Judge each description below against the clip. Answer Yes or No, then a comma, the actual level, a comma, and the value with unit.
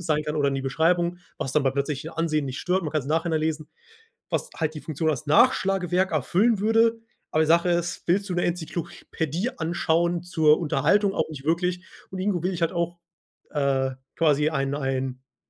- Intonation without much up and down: No, average, 3.0 semitones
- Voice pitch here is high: No, medium, 160 Hz